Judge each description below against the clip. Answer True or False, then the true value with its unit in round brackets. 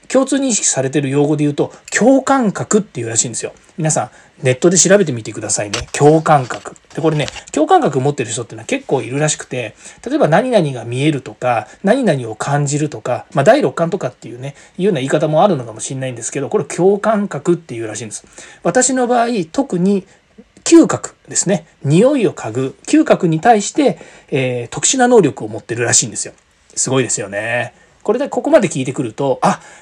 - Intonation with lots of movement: True (8.0 semitones)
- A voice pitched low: False (160 Hz)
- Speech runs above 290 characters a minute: True (415 characters per minute)